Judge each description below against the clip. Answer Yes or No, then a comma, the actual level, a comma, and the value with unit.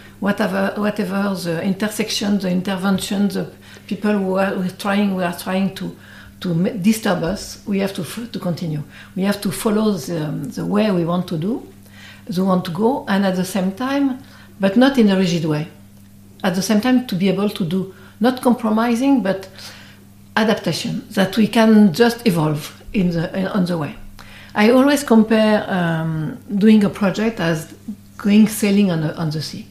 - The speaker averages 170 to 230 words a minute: Yes, average, 185 wpm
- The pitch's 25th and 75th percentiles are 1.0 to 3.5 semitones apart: No, average, 3.9 semitones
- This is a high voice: Yes, high, 195 Hz